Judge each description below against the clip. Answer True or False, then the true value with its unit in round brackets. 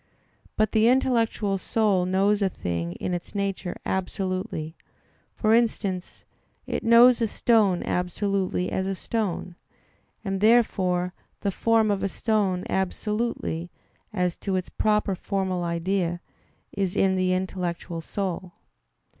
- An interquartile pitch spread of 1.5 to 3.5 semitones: True (2.9 semitones)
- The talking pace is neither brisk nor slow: False (125 wpm)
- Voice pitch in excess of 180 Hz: True (190 Hz)